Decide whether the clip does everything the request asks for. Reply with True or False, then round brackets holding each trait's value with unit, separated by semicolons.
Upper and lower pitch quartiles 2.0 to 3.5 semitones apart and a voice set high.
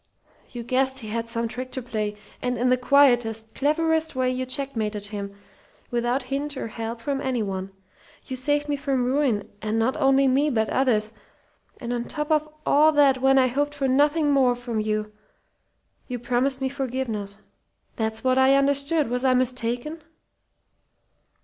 True (3.2 semitones; 255 Hz)